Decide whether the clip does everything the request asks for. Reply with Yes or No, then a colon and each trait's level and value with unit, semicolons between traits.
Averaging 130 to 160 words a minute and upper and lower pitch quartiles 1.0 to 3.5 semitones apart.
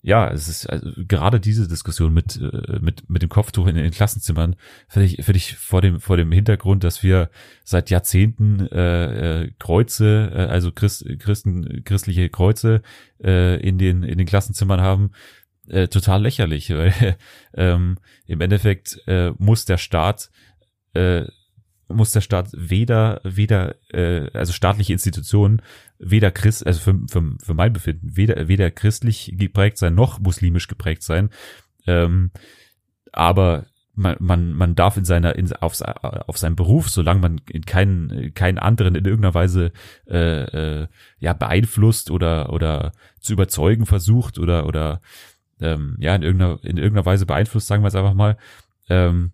Yes: average, 155 wpm; average, 3.0 semitones